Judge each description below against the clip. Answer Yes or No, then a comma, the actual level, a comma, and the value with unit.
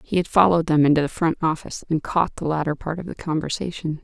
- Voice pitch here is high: No, medium, 160 Hz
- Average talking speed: No, fast, 240 wpm